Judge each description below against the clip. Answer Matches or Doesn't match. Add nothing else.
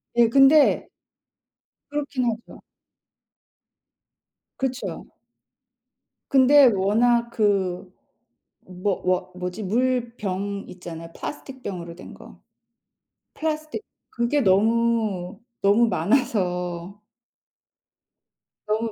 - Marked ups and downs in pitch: Doesn't match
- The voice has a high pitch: Matches